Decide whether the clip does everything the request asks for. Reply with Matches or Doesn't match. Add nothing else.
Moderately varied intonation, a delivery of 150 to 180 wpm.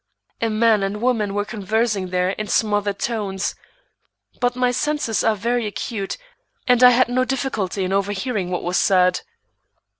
Matches